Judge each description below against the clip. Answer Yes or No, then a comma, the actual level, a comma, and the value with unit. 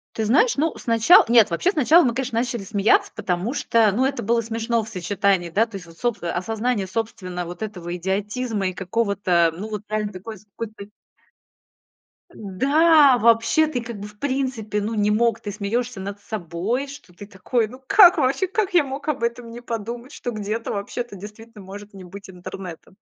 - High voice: Yes, high, 220 Hz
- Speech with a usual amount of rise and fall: Yes, average, 3.7 semitones